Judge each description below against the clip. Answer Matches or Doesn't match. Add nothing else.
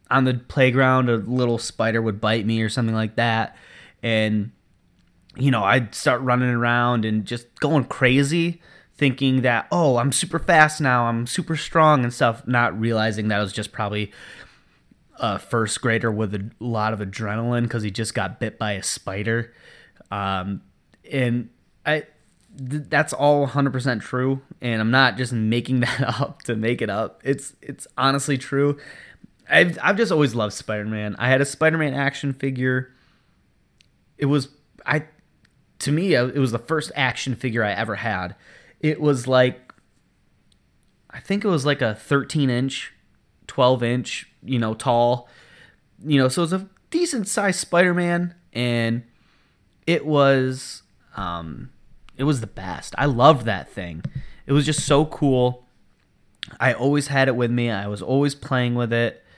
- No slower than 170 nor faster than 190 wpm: Doesn't match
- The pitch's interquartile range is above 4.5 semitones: Doesn't match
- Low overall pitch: Matches